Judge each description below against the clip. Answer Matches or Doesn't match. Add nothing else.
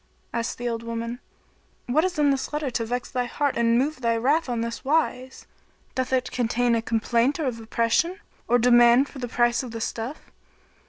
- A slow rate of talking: Doesn't match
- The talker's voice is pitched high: Matches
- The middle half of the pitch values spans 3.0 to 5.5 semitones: Doesn't match